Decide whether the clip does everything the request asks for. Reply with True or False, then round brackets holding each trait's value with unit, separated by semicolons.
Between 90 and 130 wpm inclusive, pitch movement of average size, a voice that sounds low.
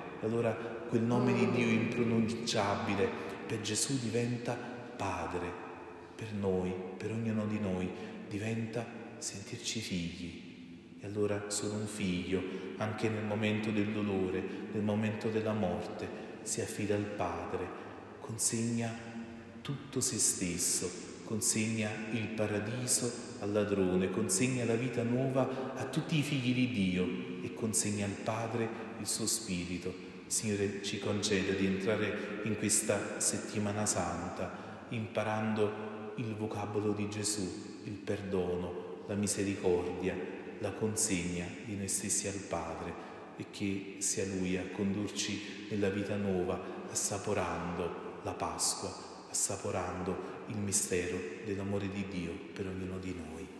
True (125 wpm; 3.0 semitones; 105 Hz)